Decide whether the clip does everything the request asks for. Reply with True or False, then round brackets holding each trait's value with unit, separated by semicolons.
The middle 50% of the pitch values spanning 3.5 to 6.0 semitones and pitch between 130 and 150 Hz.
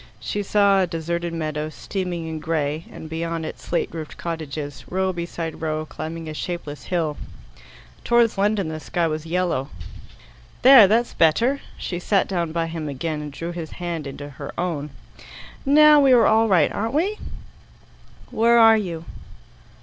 False (4.2 semitones; 170 Hz)